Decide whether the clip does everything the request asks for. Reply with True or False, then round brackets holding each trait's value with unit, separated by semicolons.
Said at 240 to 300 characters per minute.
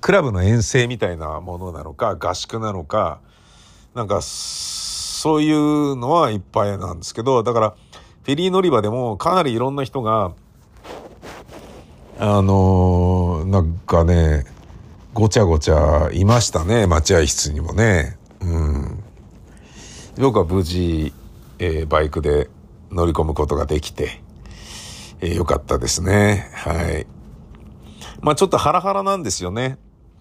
True (255 characters per minute)